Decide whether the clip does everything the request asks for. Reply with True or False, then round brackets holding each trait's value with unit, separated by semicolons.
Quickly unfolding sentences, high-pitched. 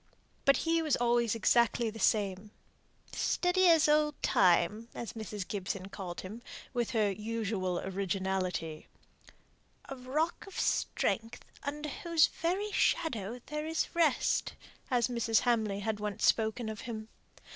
False (135 wpm; 230 Hz)